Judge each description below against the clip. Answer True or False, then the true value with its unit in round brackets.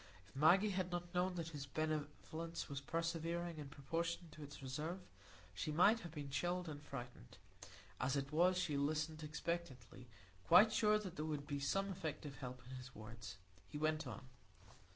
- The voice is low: False (155 Hz)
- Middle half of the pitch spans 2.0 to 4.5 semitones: True (3.7 semitones)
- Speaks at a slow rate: False (175 wpm)